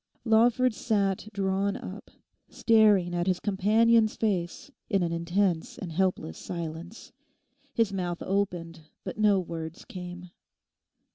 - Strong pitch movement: No, average, 3.4 semitones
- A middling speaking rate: No, slow, 120 wpm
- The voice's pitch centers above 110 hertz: Yes, high, 190 Hz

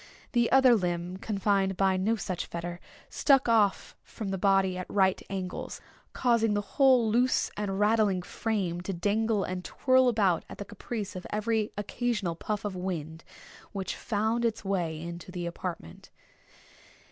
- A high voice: Yes, high, 200 Hz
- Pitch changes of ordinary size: Yes, average, 3.5 semitones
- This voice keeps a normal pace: Yes, average, 155 wpm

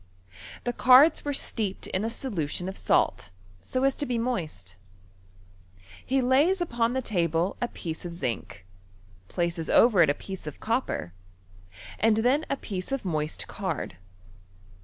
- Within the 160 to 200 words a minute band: No, average, 150 wpm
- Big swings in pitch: Yes, wide, 7.2 semitones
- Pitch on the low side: No, high, 210 Hz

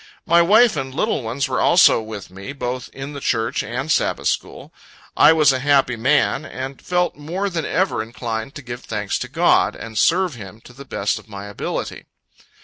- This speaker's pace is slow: No, average, 195 wpm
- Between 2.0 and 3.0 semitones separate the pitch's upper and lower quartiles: No, wide, 5.6 semitones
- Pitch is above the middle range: No, low, 135 Hz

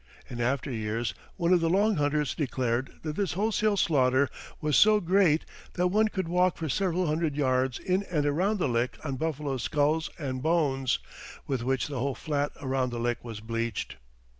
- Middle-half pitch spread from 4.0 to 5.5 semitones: Yes, average, 5.2 semitones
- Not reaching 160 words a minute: No, average, 185 wpm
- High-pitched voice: No, medium, 145 Hz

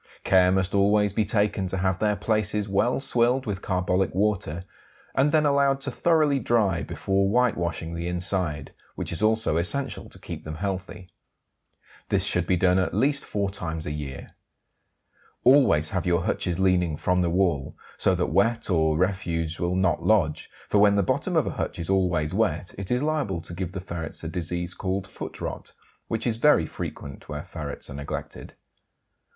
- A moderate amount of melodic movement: Yes, average, 3.8 semitones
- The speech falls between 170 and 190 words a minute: Yes, average, 180 wpm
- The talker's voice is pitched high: No, very low, 95 Hz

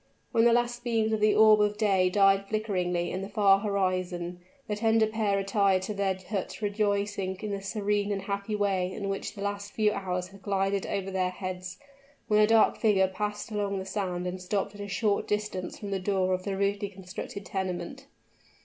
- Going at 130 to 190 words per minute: No, average, 200 wpm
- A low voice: No, high, 200 Hz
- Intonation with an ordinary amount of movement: No, narrow, 1.8 semitones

